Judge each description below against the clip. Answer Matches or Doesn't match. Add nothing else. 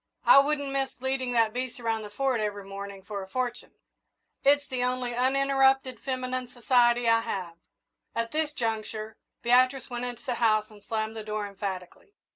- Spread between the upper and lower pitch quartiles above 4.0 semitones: Doesn't match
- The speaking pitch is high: Matches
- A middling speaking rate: Matches